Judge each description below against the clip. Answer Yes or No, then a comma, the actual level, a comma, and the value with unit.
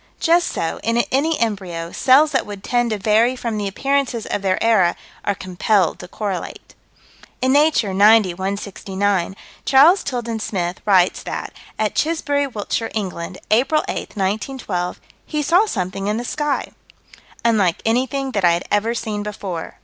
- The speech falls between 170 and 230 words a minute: No, average, 155 wpm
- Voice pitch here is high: Yes, high, 215 Hz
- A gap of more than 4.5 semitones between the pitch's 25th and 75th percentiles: Yes, average, 5.3 semitones